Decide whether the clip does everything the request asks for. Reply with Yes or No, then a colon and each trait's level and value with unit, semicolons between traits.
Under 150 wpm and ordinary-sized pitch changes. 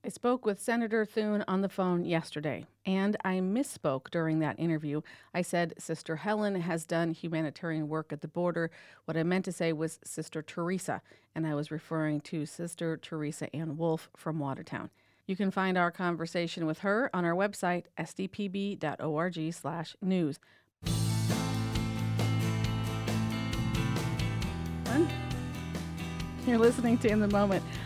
Yes: average, 140 wpm; average, 4.1 semitones